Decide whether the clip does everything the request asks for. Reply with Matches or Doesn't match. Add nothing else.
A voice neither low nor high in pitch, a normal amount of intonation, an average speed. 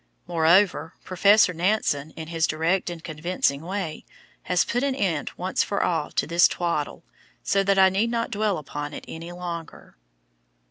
Matches